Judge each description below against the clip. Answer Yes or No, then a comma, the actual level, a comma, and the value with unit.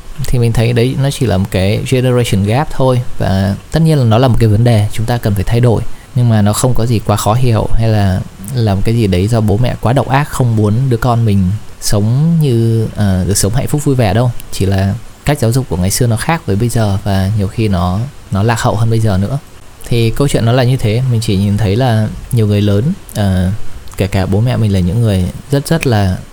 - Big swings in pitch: No, average, 3.7 semitones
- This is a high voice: No, low, 115 Hz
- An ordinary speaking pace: No, fast, 260 wpm